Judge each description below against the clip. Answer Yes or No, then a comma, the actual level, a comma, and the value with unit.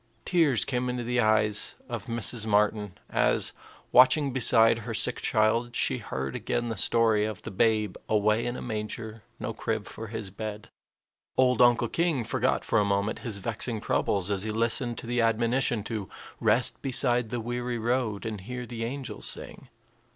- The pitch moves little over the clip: Yes, narrow, 2.3 semitones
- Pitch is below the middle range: Yes, low, 115 Hz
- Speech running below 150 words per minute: No, average, 175 wpm